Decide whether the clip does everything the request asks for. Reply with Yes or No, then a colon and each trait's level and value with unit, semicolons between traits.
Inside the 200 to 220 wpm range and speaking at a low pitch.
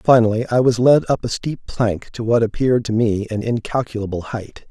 Yes: fast, 205 wpm; low, 115 Hz